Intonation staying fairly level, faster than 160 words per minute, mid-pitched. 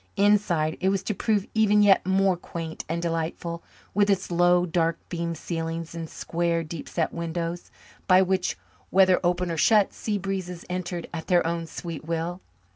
Yes: narrow, 2.3 semitones; average, 170 wpm; medium, 175 Hz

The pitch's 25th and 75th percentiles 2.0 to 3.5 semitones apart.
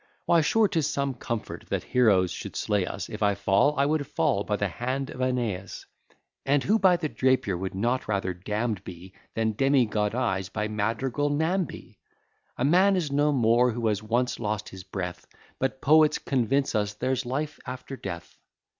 No: average, 5.2 semitones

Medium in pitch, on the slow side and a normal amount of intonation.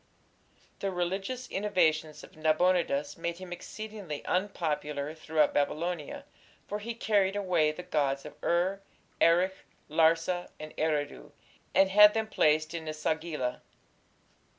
Yes: medium, 170 Hz; slow, 125 wpm; average, 3.8 semitones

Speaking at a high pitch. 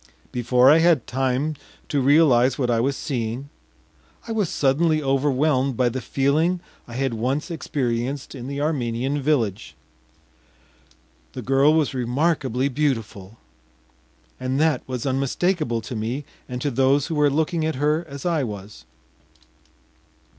No: low, 135 Hz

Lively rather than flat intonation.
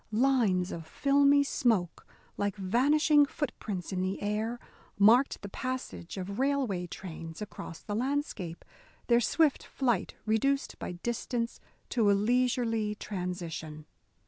Yes: wide, 5.7 semitones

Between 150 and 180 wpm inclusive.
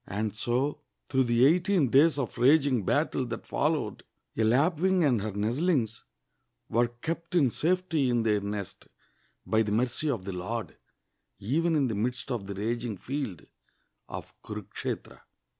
Yes: average, 155 wpm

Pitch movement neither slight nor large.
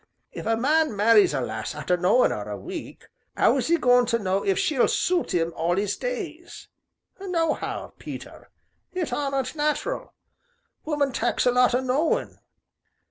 No: wide, 7.7 semitones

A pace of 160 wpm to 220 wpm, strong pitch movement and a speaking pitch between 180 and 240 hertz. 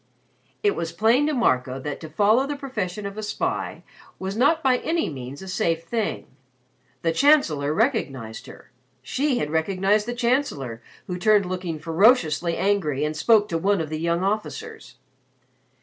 Yes: average, 165 wpm; wide, 7.1 semitones; high, 190 Hz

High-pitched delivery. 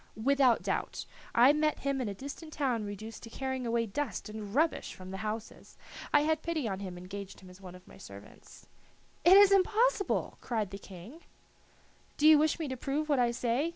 Yes: high, 245 Hz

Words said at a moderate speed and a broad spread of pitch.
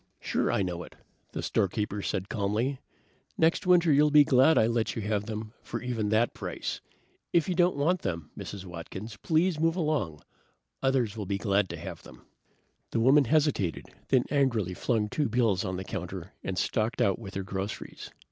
Yes: average, 185 wpm; wide, 6.4 semitones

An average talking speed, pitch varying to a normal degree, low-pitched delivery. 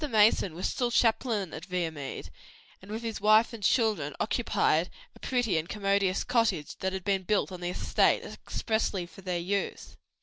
No: average, 170 wpm; average, 3.4 semitones; high, 200 Hz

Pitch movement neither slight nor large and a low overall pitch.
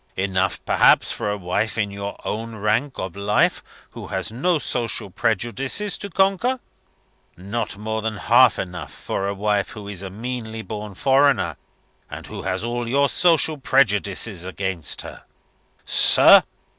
Yes: average, 4.2 semitones; low, 110 Hz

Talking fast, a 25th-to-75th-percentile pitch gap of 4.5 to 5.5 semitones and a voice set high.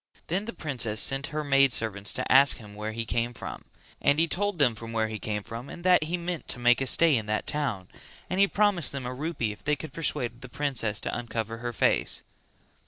No: fast, 230 wpm; average, 5.2 semitones; low, 130 Hz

